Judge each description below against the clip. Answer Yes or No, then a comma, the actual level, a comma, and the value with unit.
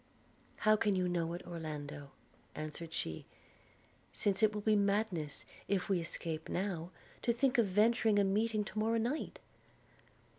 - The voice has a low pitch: No, high, 200 Hz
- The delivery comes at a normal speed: Yes, average, 150 wpm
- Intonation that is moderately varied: Yes, average, 4.4 semitones